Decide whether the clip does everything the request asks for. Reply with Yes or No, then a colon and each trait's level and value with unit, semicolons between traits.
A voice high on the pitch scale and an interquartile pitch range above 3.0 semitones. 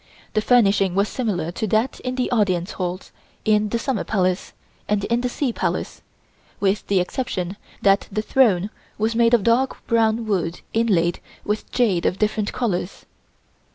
Yes: high, 215 Hz; average, 3.5 semitones